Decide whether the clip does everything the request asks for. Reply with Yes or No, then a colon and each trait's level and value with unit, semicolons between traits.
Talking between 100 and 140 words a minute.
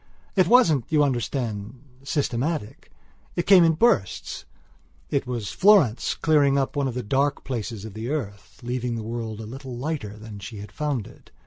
No: average, 175 wpm